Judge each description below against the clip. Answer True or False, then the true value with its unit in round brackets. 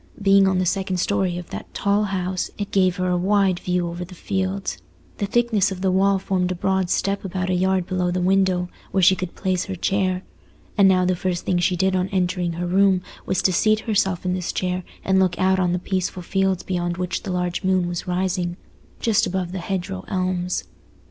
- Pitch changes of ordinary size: False (1.2 semitones)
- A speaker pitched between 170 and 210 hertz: True (185 Hz)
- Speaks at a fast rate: True (215 wpm)